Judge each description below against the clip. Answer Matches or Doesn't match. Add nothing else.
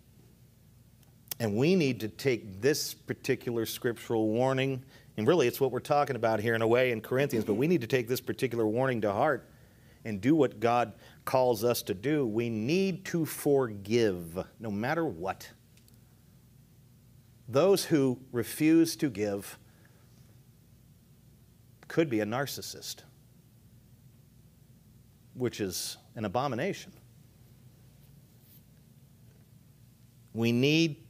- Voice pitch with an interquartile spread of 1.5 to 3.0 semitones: Matches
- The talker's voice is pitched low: Matches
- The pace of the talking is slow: Matches